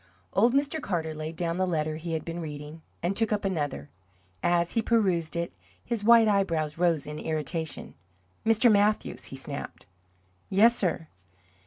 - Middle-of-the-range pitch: Yes, medium, 170 Hz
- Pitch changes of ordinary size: Yes, average, 5.0 semitones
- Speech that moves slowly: No, average, 160 wpm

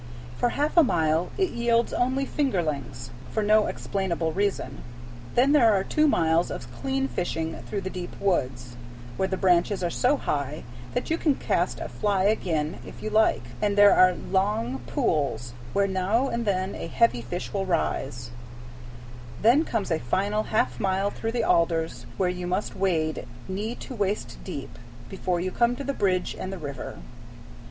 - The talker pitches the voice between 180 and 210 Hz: Yes, high, 190 Hz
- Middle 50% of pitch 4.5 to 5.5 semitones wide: Yes, average, 5.1 semitones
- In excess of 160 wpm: Yes, average, 175 wpm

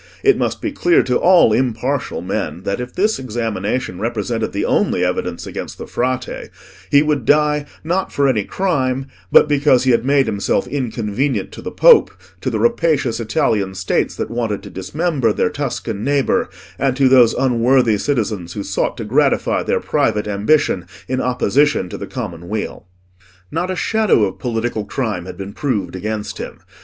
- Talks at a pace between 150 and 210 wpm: Yes, average, 170 wpm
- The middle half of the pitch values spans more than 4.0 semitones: Yes, average, 5.2 semitones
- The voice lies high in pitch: No, low, 120 Hz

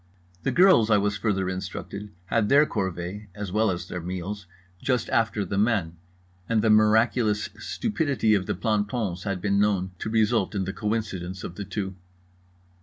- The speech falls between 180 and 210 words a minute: No, average, 170 wpm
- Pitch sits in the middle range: No, low, 105 Hz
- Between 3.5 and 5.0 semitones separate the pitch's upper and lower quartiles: No, average, 2.8 semitones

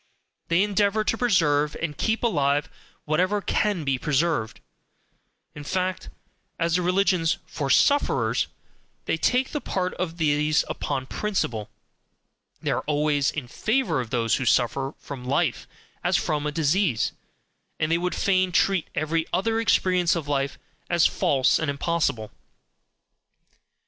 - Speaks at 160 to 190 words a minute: No, average, 140 wpm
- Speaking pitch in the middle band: Yes, medium, 160 Hz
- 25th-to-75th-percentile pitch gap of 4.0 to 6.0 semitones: Yes, average, 4.5 semitones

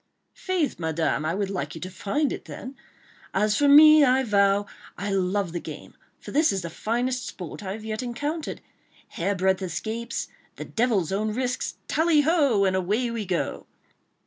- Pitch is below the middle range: No, high, 215 Hz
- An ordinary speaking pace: Yes, average, 165 wpm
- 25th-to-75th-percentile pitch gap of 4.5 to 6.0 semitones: Yes, wide, 5.4 semitones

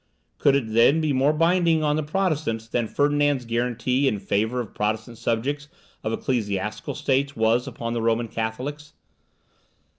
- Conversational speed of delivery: Yes, average, 150 wpm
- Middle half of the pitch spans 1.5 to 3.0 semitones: No, average, 4.5 semitones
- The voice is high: No, low, 125 Hz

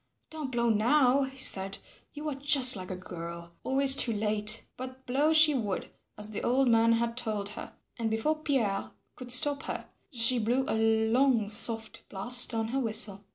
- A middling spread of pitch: Yes, average, 3.9 semitones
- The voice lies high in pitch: Yes, high, 235 Hz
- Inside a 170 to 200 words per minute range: Yes, average, 180 wpm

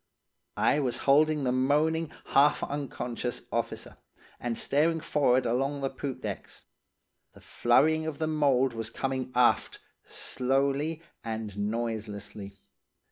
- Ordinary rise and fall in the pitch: Yes, average, 3.7 semitones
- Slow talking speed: Yes, slow, 120 wpm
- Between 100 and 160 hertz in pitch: Yes, low, 135 Hz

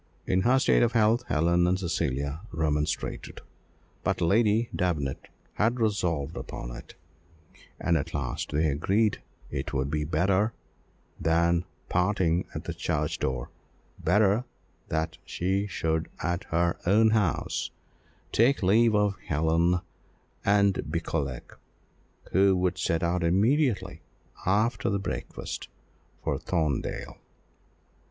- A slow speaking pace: Yes, slow, 115 wpm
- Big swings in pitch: No, average, 4.4 semitones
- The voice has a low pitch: Yes, very low, 90 Hz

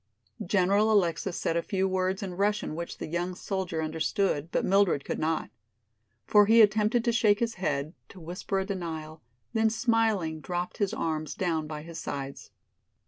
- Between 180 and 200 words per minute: No, average, 170 wpm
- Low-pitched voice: No, medium, 185 Hz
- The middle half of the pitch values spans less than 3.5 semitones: No, average, 4.3 semitones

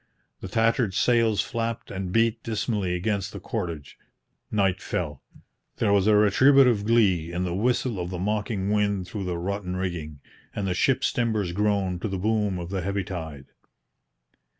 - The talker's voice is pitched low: Yes, low, 100 Hz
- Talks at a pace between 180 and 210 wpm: No, average, 165 wpm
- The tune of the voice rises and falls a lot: No, average, 3.4 semitones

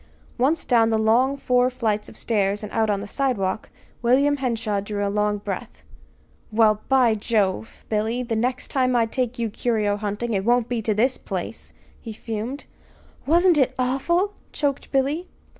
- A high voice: Yes, high, 230 Hz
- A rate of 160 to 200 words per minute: Yes, average, 170 wpm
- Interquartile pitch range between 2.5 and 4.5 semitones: Yes, average, 3.4 semitones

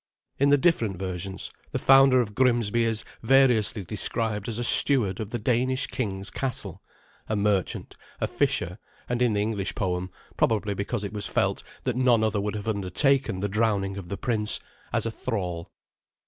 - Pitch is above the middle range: No, low, 110 Hz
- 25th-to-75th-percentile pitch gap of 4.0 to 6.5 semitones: No, average, 3.6 semitones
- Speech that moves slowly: No, average, 175 wpm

